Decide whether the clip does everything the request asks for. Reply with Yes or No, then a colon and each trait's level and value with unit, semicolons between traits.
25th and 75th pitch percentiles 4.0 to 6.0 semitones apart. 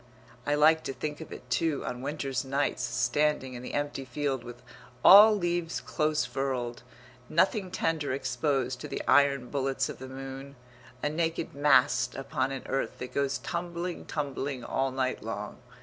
No: average, 2.7 semitones